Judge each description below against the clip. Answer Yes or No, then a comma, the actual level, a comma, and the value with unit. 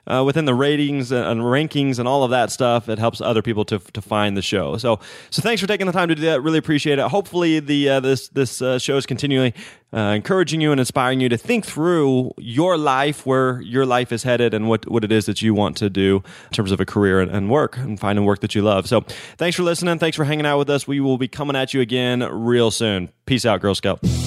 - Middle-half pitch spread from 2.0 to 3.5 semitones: No, average, 4.7 semitones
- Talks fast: Yes, fast, 260 wpm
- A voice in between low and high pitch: No, low, 125 Hz